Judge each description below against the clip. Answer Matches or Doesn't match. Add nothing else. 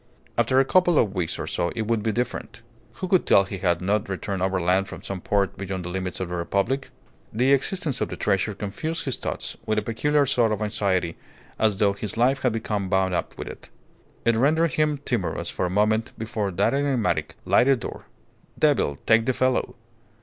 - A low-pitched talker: Matches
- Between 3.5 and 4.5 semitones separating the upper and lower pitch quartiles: Doesn't match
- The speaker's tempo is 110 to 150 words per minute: Doesn't match